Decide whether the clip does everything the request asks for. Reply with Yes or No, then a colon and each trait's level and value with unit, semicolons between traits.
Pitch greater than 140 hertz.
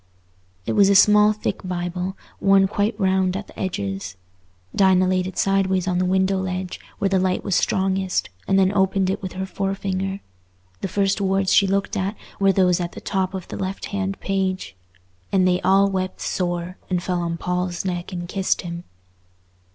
Yes: high, 190 Hz